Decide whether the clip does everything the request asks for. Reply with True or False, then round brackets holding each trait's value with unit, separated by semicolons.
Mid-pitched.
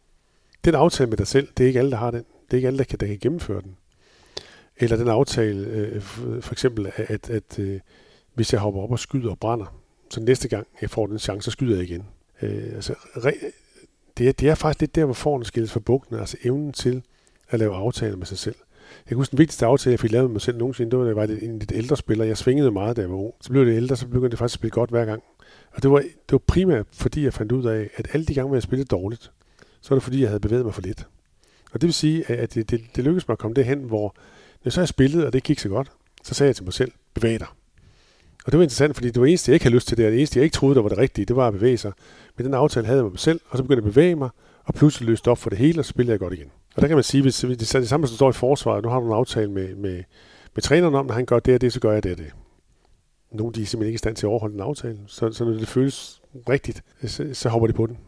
False (120 Hz)